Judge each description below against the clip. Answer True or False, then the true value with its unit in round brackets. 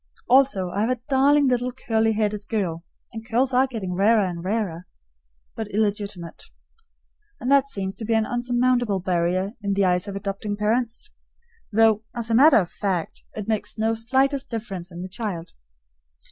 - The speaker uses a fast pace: False (170 wpm)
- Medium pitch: False (215 Hz)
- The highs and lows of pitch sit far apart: False (3.9 semitones)